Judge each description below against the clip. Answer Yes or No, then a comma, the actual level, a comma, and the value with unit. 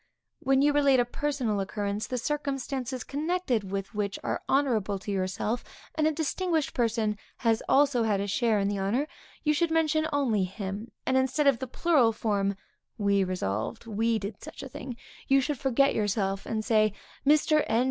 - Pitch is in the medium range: No, high, 235 Hz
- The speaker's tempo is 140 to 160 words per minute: No, average, 175 wpm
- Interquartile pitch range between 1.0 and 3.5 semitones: No, wide, 5.5 semitones